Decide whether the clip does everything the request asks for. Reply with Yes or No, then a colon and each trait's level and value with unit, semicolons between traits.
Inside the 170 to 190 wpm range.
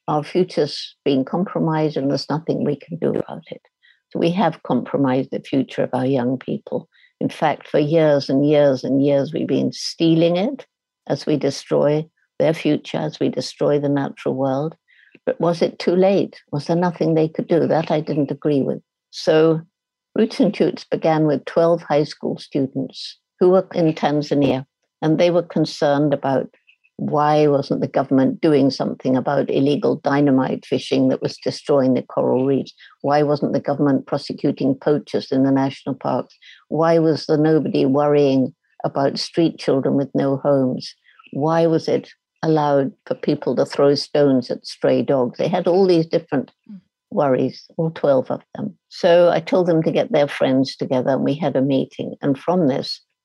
Yes: average, 175 wpm